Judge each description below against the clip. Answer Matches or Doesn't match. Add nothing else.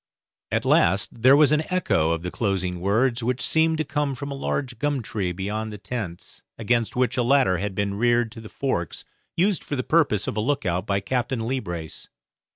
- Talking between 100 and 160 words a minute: Doesn't match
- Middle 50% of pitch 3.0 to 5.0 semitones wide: Doesn't match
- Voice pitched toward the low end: Matches